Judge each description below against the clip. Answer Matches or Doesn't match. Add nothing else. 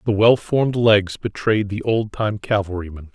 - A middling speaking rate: Matches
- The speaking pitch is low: Matches